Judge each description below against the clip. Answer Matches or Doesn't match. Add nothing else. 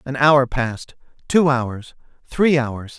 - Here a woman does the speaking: Doesn't match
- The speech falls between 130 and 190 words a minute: Matches